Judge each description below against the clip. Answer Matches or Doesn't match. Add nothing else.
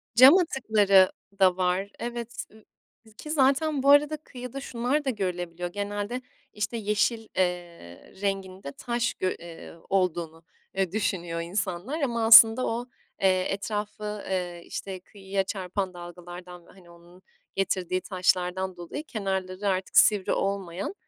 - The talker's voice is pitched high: Matches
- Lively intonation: Doesn't match